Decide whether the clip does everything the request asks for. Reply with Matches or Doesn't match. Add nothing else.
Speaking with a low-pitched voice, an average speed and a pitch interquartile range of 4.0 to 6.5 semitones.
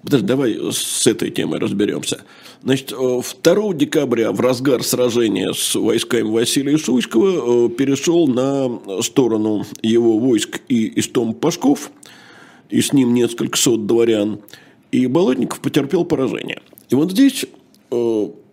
Matches